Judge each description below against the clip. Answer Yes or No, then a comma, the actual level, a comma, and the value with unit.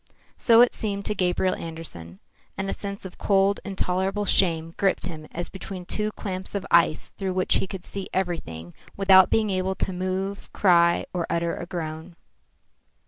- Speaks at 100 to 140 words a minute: No, average, 175 wpm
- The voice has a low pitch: No, medium, 185 Hz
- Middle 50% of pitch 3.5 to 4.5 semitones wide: No, narrow, 2.4 semitones